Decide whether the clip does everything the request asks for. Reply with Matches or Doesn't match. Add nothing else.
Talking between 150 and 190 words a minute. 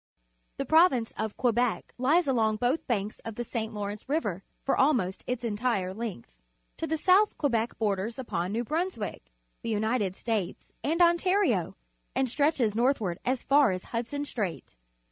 Matches